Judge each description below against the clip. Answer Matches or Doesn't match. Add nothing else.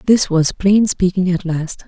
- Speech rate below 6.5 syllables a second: Matches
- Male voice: Doesn't match